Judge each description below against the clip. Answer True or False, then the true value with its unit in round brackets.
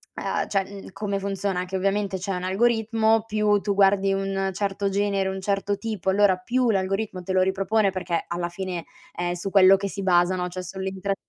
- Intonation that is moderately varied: False (1.5 semitones)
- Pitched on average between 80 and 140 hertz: False (195 Hz)